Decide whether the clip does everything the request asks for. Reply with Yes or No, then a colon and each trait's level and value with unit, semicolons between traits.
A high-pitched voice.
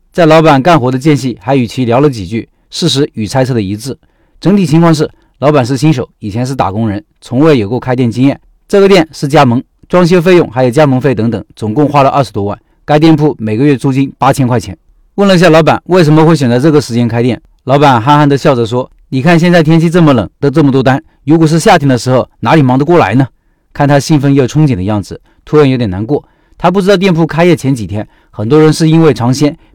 No: medium, 140 Hz